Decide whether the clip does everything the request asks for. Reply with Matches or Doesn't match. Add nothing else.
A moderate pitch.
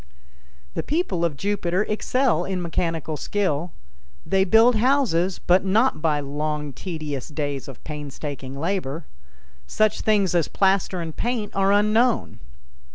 Matches